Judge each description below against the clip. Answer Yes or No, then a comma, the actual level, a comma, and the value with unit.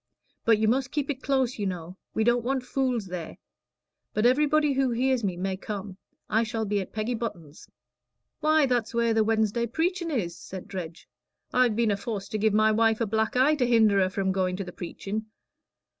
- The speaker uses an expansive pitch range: No, average, 4.1 semitones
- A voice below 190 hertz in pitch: No, high, 220 Hz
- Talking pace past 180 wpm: Yes, average, 200 wpm